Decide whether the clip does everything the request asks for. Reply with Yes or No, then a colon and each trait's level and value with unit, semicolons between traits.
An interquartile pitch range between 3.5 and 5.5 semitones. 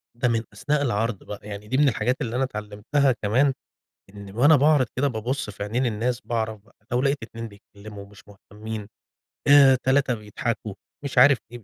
Yes: average, 4.1 semitones